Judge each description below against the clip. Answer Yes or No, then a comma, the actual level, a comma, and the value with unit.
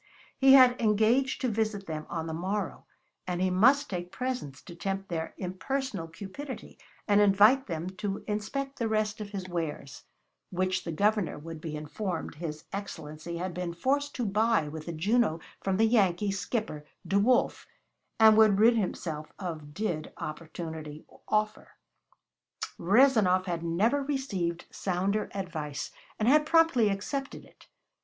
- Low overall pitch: No, high, 195 Hz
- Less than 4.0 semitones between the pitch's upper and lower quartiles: No, average, 4.8 semitones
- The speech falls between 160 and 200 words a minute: No, average, 150 wpm